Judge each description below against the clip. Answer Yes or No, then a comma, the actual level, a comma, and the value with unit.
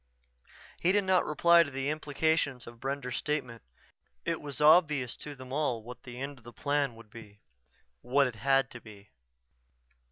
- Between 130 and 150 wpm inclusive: No, average, 170 wpm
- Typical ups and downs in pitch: Yes, average, 3.8 semitones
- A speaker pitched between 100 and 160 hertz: Yes, low, 135 Hz